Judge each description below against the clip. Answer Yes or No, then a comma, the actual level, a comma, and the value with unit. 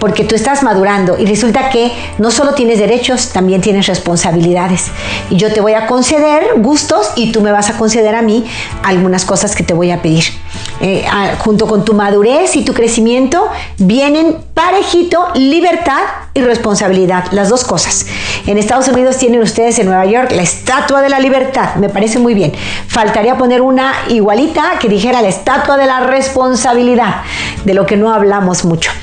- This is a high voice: Yes, high, 225 Hz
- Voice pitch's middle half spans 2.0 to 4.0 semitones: No, average, 4.7 semitones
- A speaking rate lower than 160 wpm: No, average, 180 wpm